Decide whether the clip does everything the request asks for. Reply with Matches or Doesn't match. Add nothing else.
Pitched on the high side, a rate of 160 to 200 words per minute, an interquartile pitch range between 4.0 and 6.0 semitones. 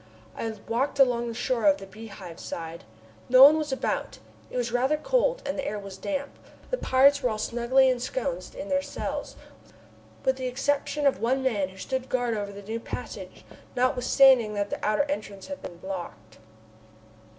Matches